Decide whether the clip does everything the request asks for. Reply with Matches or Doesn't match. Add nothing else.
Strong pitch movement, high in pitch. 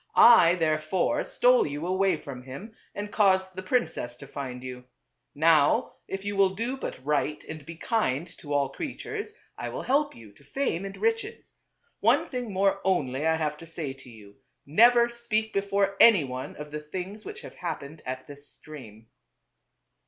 Doesn't match